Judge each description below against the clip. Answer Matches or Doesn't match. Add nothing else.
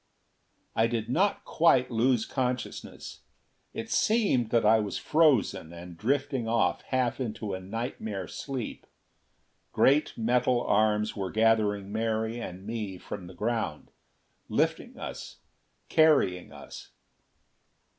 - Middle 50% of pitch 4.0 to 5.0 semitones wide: Doesn't match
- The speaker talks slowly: Matches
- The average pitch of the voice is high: Doesn't match